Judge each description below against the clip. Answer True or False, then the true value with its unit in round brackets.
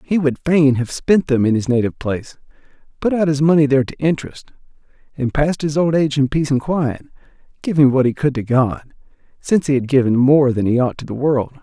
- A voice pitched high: False (140 Hz)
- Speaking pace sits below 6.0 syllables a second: False (6.1 syllables/s)